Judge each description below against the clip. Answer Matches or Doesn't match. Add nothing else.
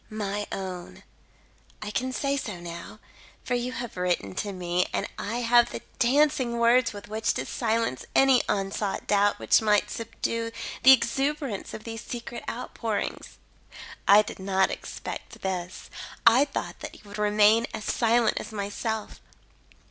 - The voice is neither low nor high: Doesn't match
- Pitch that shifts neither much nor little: Matches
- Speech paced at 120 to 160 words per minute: Matches